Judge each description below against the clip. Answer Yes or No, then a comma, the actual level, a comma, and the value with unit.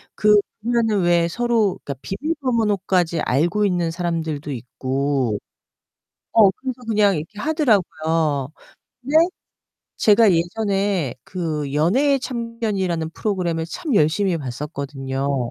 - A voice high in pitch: No, medium, 180 Hz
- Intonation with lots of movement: Yes, wide, 6.2 semitones